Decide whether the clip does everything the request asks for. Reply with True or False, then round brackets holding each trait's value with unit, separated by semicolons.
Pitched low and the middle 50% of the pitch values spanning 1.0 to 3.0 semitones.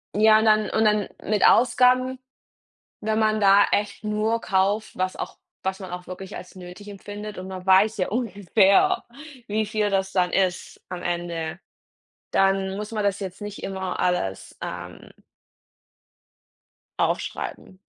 False (200 Hz; 2.4 semitones)